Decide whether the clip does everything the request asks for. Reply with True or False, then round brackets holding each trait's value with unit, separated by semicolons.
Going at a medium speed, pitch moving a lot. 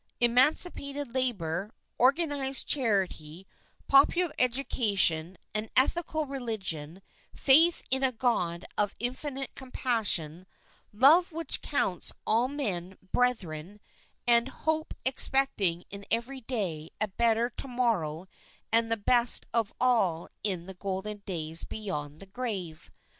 False (115 wpm; 5.9 semitones)